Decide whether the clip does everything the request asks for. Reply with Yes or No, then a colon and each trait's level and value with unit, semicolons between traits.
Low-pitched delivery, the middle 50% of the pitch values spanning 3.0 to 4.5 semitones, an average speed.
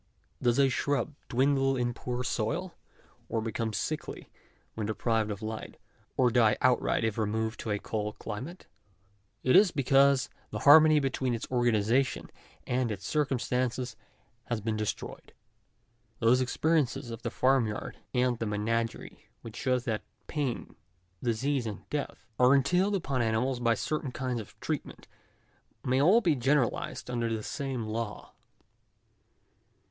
Yes: low, 125 Hz; average, 3.3 semitones; average, 145 wpm